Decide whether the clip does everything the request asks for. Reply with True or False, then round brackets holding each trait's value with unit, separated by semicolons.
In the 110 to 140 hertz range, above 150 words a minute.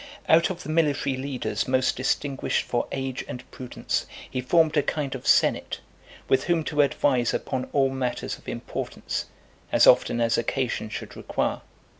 True (135 Hz; 160 wpm)